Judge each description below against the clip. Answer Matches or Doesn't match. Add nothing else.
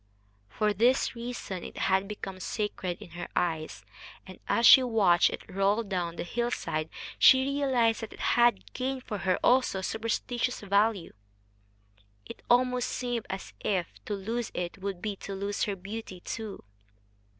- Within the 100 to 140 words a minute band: Doesn't match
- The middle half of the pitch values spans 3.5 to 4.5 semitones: Matches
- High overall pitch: Matches